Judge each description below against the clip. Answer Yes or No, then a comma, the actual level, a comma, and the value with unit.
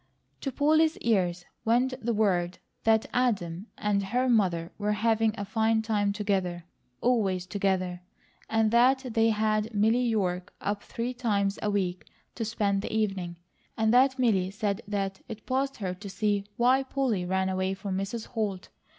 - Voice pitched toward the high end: Yes, high, 210 Hz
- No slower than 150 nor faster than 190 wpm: Yes, average, 160 wpm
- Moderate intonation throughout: Yes, average, 3.3 semitones